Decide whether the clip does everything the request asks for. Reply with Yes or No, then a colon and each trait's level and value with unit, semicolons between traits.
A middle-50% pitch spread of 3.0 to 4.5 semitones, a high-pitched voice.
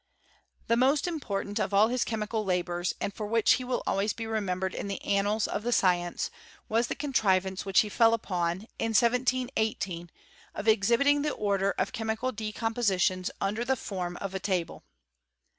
Yes: average, 3.4 semitones; high, 210 Hz